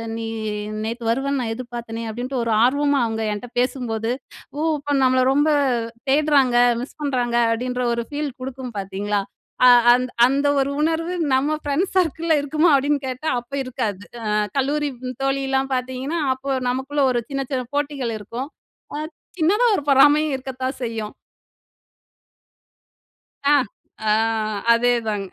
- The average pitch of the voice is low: No, very high, 265 Hz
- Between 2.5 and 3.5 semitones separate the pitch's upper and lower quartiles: Yes, average, 3.1 semitones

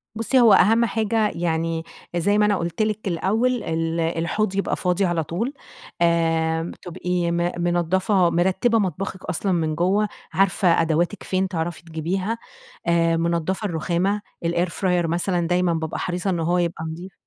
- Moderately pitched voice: Yes, medium, 175 Hz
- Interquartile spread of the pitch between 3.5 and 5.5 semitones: No, average, 2.8 semitones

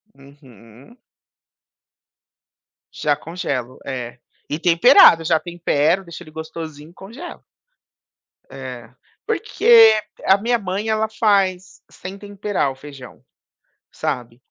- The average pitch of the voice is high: No, medium, 165 Hz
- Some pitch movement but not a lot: No, wide, 6.4 semitones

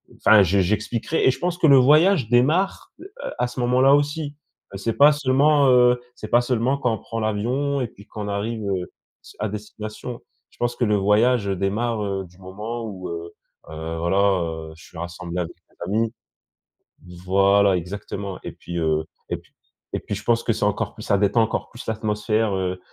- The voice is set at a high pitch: No, low, 110 Hz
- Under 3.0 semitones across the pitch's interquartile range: No, average, 4.1 semitones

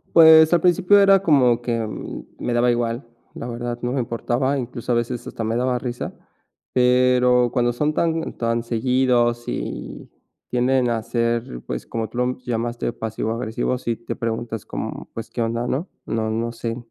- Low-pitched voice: Yes, low, 120 Hz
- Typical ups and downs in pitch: No, narrow, 1.5 semitones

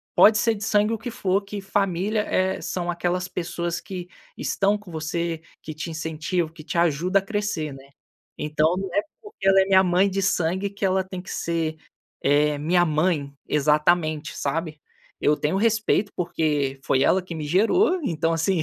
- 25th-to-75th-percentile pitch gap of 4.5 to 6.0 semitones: No, average, 3.8 semitones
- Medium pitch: Yes, medium, 175 Hz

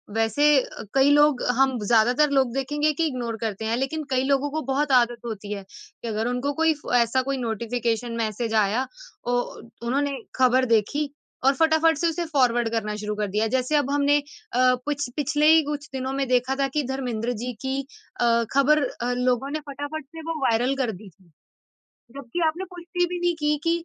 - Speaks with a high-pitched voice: Yes, very high, 265 Hz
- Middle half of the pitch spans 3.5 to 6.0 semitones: Yes, average, 4.0 semitones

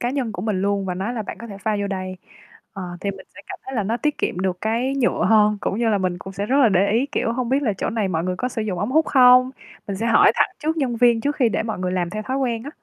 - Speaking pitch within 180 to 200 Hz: No, high, 220 Hz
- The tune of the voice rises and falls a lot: No, average, 4.3 semitones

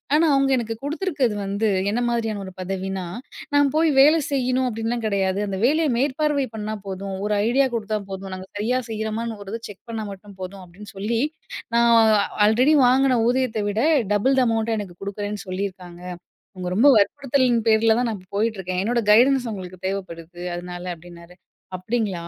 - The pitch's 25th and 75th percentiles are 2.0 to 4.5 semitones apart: Yes, average, 4.2 semitones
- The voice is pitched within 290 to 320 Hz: No, high, 215 Hz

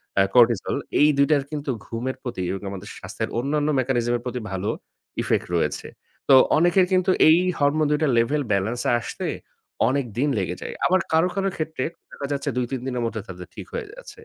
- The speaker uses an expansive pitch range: No, average, 4.9 semitones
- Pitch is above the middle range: No, low, 135 Hz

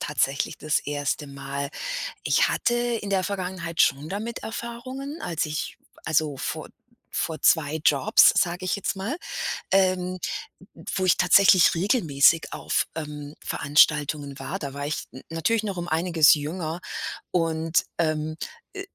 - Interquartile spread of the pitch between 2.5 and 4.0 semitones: No, average, 4.4 semitones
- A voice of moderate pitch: Yes, medium, 165 Hz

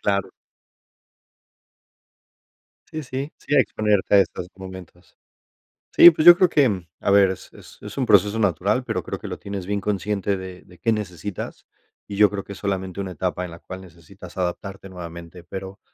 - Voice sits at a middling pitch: No, very low, 95 Hz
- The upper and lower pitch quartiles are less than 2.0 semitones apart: No, narrow, 2.3 semitones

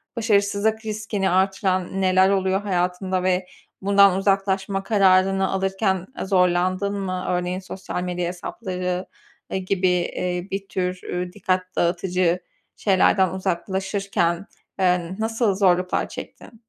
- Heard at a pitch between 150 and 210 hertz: Yes, high, 190 Hz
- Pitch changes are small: Yes, narrow, 1.5 semitones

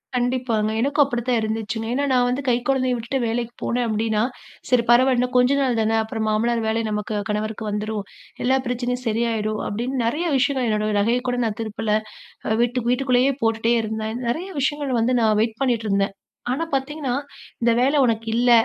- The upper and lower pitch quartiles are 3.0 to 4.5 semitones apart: No, narrow, 2.5 semitones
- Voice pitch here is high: Yes, high, 235 Hz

